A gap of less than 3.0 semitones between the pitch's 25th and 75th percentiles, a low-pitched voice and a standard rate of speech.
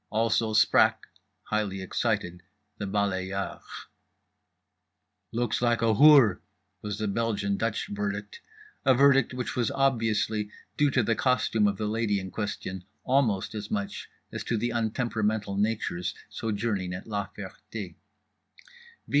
No: narrow, 2.4 semitones; low, 105 Hz; slow, 130 wpm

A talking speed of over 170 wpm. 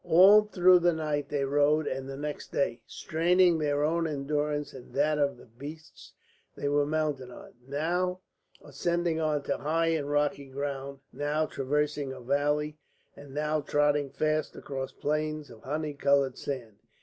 No: average, 160 wpm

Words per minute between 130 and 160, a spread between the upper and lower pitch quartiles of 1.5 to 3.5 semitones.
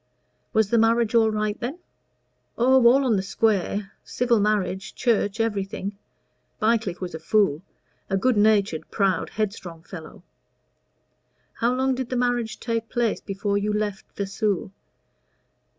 Yes: slow, 135 wpm; average, 3.1 semitones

